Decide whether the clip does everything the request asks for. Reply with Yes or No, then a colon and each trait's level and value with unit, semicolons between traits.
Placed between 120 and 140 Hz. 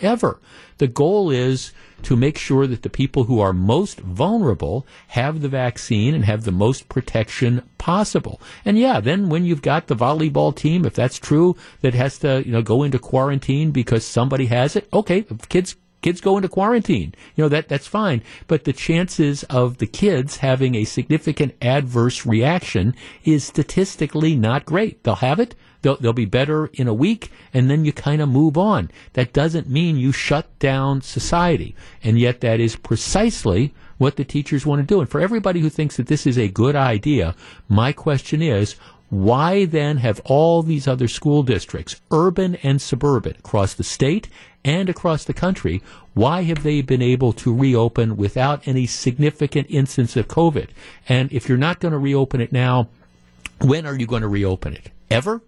Yes: low, 135 Hz